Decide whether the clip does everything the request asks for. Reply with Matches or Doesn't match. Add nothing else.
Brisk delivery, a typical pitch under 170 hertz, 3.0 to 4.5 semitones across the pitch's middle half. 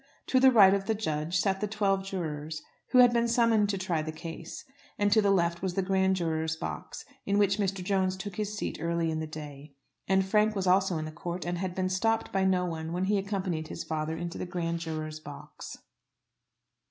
Doesn't match